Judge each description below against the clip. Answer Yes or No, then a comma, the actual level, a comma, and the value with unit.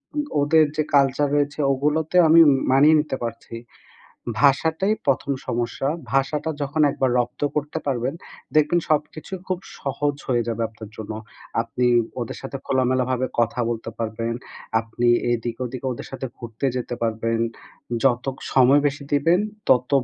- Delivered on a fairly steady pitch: No, average, 3.7 semitones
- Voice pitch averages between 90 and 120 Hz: No, low, 135 Hz